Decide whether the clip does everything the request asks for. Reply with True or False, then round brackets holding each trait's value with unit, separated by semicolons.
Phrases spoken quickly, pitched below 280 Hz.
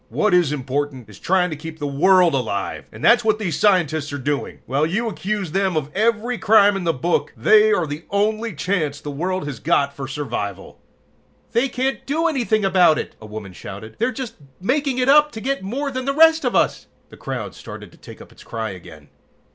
True (210 wpm; 185 Hz)